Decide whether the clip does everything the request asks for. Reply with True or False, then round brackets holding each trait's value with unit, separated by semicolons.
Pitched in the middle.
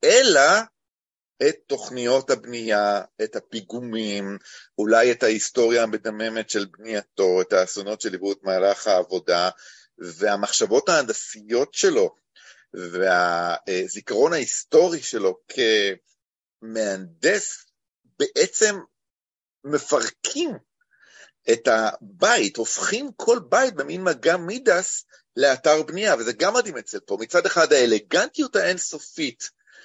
True (155 Hz)